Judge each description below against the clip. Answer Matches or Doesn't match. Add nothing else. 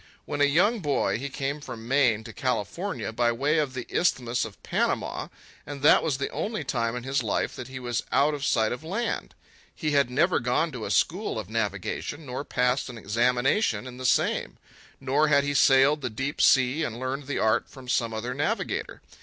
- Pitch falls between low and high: Doesn't match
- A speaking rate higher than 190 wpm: Matches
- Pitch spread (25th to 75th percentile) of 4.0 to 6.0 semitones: Doesn't match